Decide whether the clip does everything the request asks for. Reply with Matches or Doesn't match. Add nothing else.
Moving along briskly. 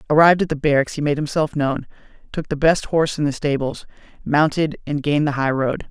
Matches